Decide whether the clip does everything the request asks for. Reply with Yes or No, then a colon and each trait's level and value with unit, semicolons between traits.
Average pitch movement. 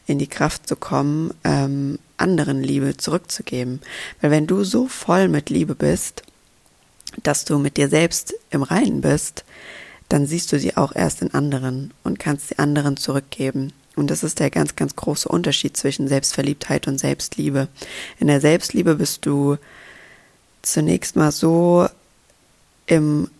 Yes: average, 3.0 semitones